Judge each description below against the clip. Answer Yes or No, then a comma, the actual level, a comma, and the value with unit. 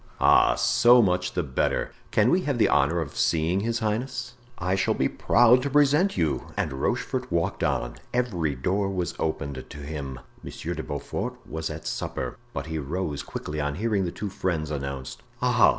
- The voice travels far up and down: Yes, wide, 7.8 semitones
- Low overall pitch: Yes, very low, 85 Hz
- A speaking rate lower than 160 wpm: No, average, 180 wpm